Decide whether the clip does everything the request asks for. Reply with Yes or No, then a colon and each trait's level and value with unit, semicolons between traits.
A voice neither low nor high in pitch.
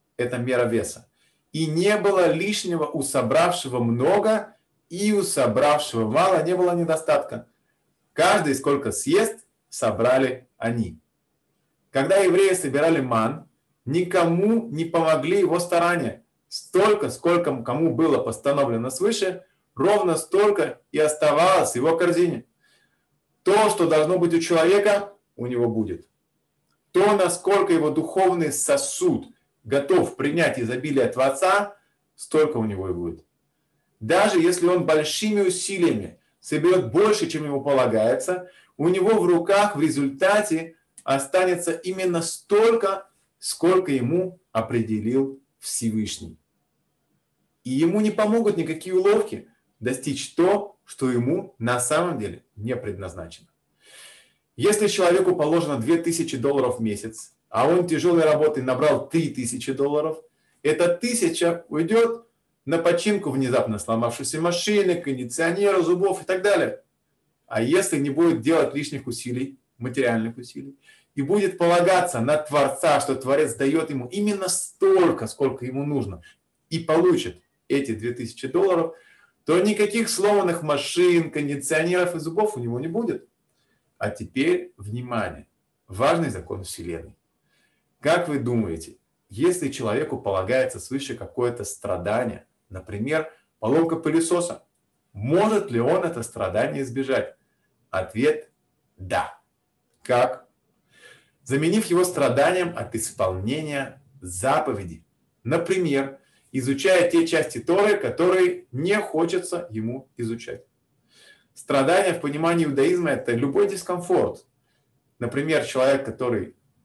Yes: medium, 160 Hz